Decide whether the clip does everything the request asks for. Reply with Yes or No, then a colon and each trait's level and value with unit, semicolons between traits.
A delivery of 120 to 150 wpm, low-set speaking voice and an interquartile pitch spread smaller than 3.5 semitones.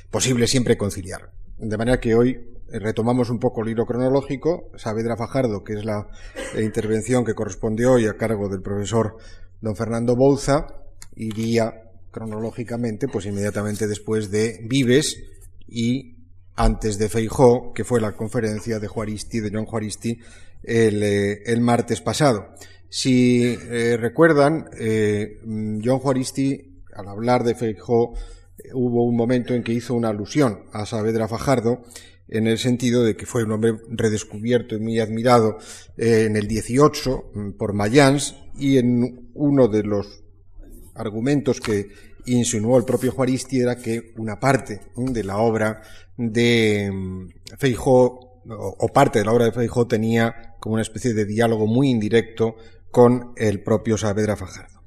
Yes: average, 145 wpm; low, 115 Hz; narrow, 2.6 semitones